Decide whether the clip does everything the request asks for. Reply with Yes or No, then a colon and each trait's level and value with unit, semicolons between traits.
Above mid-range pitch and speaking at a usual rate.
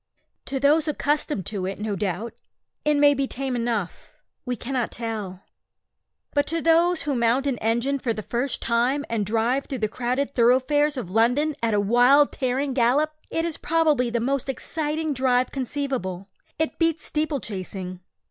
Yes: very high, 255 Hz; average, 165 wpm